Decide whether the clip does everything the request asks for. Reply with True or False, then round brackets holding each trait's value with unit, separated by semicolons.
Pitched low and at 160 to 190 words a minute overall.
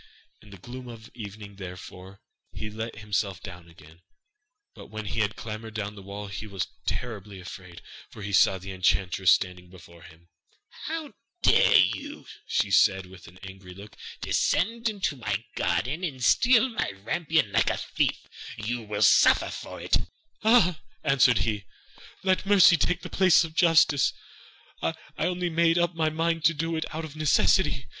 True (110 Hz; 165 wpm)